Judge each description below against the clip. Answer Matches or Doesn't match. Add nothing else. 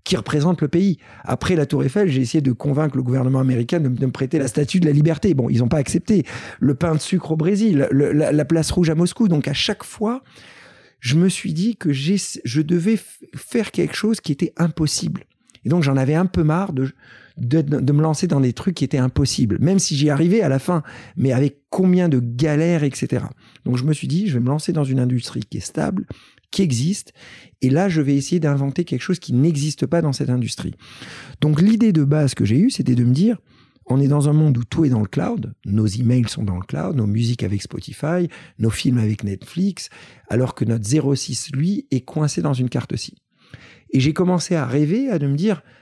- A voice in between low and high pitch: Matches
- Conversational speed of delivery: Doesn't match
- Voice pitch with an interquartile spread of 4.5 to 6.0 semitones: Matches